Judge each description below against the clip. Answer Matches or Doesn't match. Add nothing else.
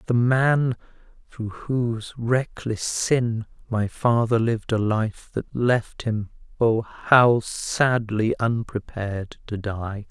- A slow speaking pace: Matches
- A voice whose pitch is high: Doesn't match